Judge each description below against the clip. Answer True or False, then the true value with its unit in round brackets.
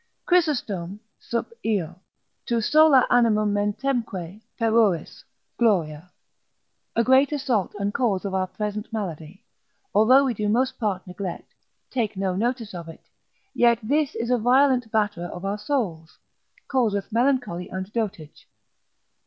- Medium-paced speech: False (130 wpm)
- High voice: True (215 Hz)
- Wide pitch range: False (4.5 semitones)